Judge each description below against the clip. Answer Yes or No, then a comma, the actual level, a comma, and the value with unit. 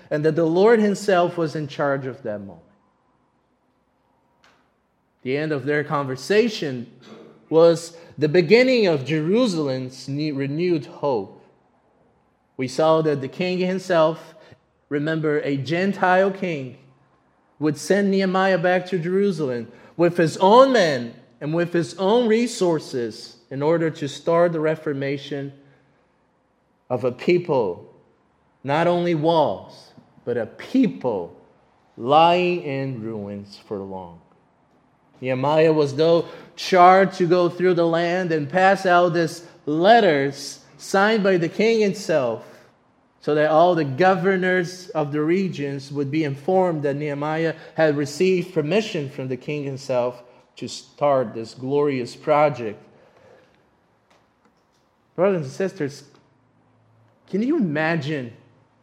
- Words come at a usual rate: No, slow, 120 wpm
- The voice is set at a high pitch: No, medium, 155 Hz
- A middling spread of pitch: Yes, average, 4.6 semitones